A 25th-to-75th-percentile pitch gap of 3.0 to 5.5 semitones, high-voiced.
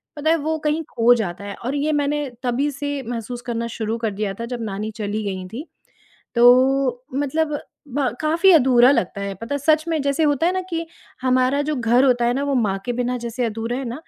Yes: average, 3.9 semitones; very high, 255 Hz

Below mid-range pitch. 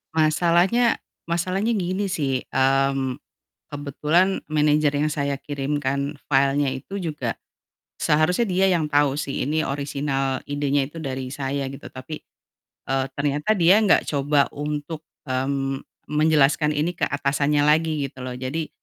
No: medium, 145 Hz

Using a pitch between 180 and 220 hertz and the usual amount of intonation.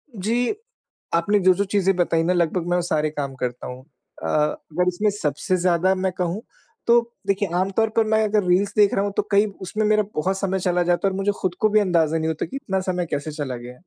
Yes: medium, 185 Hz; average, 3.6 semitones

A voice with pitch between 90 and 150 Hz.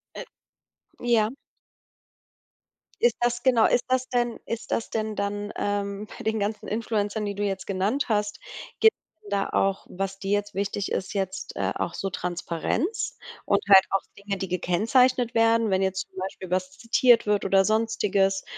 No: high, 205 Hz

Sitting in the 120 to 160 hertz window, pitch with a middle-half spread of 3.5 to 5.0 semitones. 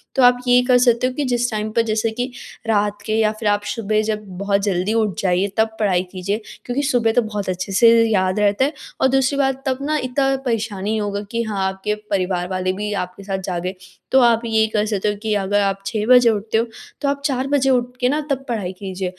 No: high, 215 Hz; average, 3.8 semitones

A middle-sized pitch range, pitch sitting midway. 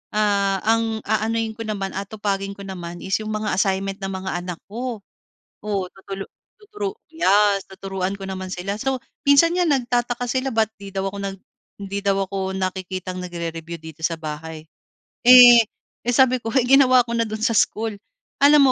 No: average, 3.6 semitones; high, 200 Hz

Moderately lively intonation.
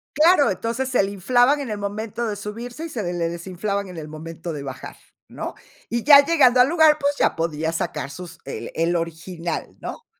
No: wide, 7.3 semitones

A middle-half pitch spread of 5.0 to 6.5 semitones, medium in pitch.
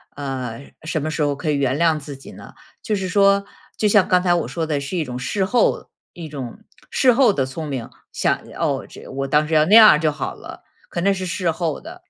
Yes: average, 5.3 semitones; medium, 160 Hz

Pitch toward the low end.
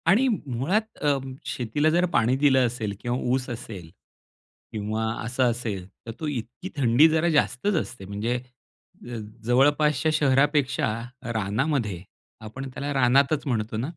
Yes: low, 130 Hz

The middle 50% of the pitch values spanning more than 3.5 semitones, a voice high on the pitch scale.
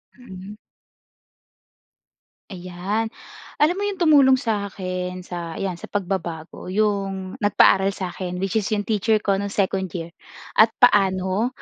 No: average, 2.8 semitones; high, 195 Hz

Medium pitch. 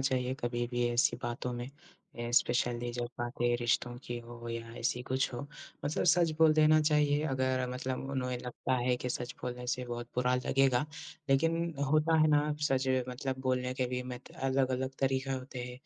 No: low, 125 Hz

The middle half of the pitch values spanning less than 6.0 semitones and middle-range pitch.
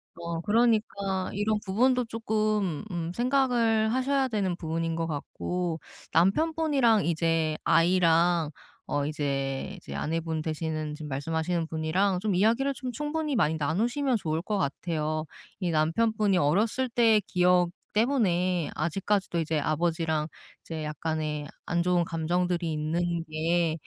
Yes: average, 5.3 semitones; medium, 175 Hz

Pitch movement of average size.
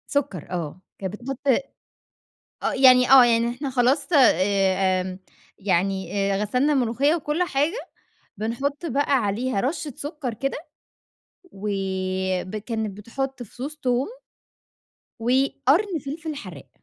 No: wide, 6.1 semitones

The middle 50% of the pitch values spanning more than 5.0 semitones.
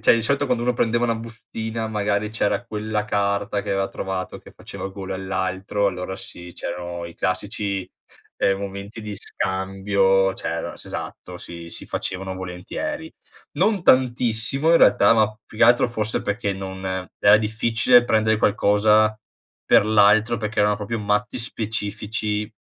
No: narrow, 2.5 semitones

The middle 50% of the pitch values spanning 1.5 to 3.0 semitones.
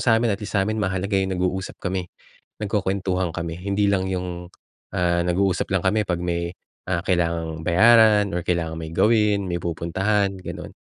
Yes: narrow, 2.5 semitones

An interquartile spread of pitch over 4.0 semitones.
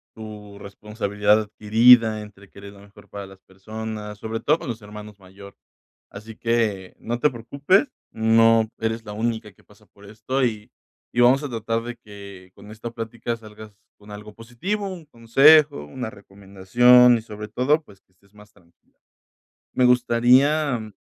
No: average, 2.8 semitones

